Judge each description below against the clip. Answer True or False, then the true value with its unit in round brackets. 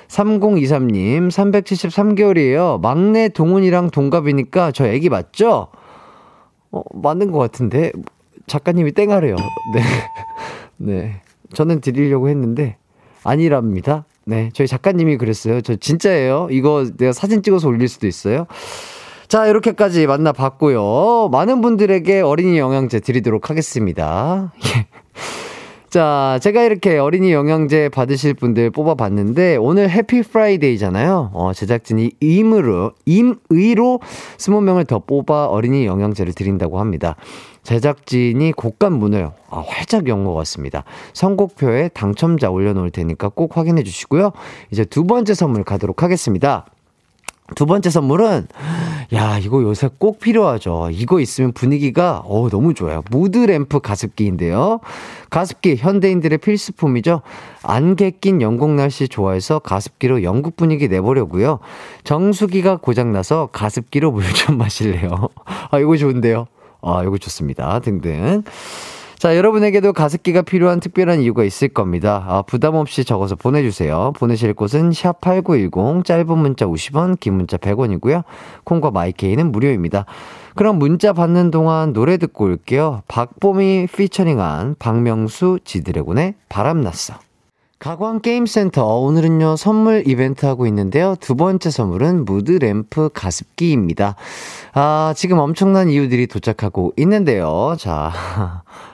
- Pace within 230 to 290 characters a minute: False (310 characters per minute)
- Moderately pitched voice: True (145 Hz)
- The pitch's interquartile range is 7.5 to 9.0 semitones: True (8.4 semitones)